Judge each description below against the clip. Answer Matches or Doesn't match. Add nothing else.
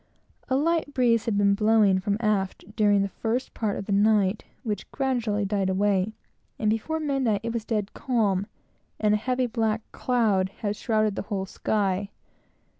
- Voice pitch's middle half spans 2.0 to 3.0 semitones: Matches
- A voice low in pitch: Doesn't match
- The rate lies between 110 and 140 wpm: Doesn't match